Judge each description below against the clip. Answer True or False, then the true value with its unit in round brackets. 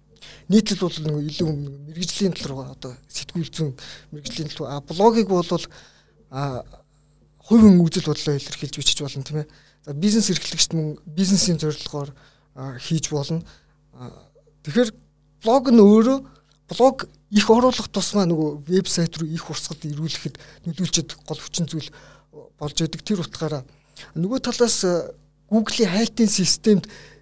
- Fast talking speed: False (125 wpm)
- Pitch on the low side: False (160 Hz)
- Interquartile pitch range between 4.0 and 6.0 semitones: True (4.6 semitones)